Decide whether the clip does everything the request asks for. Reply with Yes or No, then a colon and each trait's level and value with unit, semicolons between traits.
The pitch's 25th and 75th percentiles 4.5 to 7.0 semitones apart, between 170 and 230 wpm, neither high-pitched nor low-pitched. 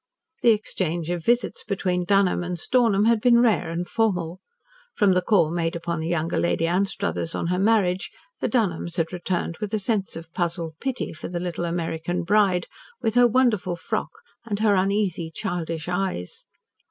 No: average, 3.8 semitones; average, 175 wpm; medium, 180 Hz